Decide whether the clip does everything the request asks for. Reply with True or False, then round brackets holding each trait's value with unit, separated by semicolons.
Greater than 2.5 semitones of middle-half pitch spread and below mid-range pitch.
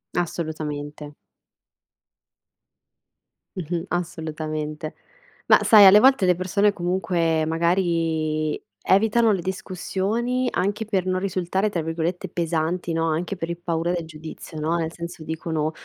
False (2.9 semitones; 170 Hz)